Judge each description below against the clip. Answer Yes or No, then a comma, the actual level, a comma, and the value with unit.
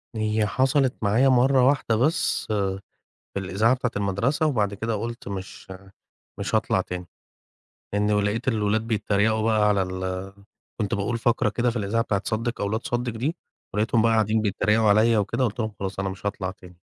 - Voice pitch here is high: No, low, 110 Hz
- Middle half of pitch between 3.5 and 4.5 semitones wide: No, average, 2.7 semitones